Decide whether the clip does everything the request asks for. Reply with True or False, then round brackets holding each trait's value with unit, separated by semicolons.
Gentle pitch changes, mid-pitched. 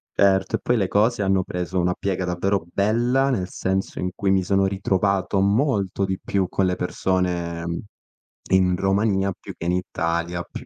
False (1.5 semitones; 95 Hz)